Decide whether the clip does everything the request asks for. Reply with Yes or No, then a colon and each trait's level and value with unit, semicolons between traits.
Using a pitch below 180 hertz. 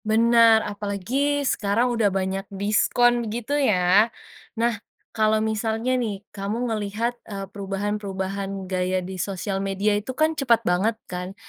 No: high, 210 Hz